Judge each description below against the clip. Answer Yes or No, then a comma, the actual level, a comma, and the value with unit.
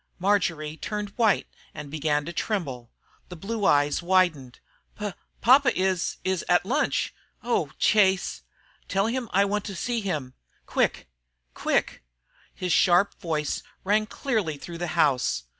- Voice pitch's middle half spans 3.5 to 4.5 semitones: No, average, 5.0 semitones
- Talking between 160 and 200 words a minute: No, average, 140 wpm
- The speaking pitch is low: No, medium, 185 Hz